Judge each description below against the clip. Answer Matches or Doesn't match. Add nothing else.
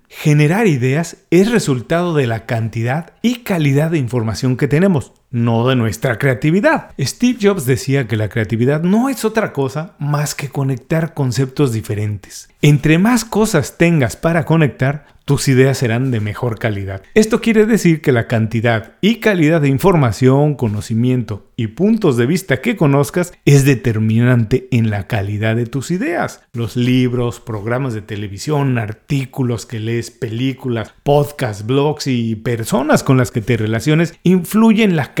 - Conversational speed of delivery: Matches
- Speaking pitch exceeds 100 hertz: Matches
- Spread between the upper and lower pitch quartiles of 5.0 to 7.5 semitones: Matches